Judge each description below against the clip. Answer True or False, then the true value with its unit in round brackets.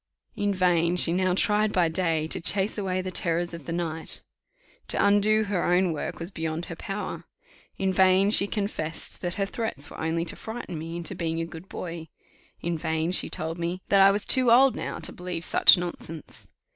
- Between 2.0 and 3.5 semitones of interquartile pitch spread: True (3.0 semitones)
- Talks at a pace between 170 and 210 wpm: True (200 wpm)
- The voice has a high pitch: False (180 Hz)